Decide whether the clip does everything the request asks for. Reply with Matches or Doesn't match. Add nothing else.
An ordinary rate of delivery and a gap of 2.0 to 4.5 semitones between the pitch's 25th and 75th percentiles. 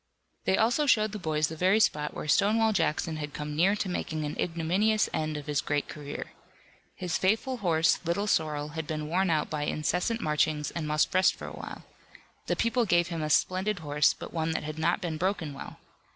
Doesn't match